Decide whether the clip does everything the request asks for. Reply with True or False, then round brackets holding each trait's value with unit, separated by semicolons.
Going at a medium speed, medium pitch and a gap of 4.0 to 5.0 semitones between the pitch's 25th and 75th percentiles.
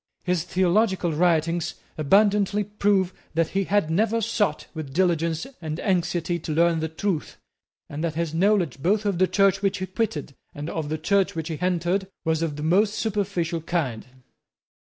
False (170 wpm; 175 Hz; 3.6 semitones)